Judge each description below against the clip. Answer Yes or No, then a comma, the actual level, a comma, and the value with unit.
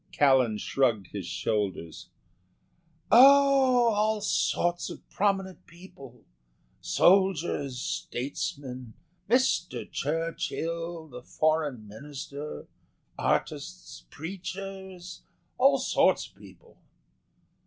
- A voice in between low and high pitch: Yes, medium, 165 Hz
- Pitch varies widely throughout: Yes, wide, 7.3 semitones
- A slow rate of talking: Yes, slow, 80 wpm